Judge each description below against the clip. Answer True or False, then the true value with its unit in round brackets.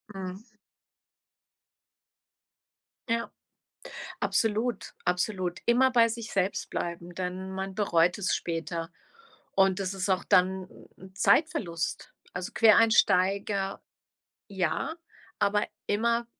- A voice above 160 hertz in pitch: True (190 Hz)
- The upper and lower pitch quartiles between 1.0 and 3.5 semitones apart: True (3.0 semitones)